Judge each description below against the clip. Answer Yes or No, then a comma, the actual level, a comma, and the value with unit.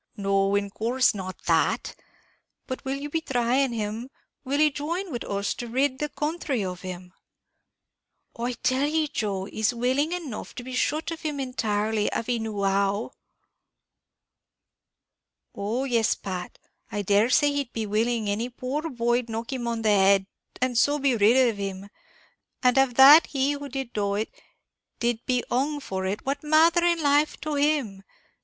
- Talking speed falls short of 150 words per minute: No, average, 170 wpm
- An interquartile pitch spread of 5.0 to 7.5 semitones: Yes, wide, 5.4 semitones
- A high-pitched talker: Yes, high, 245 Hz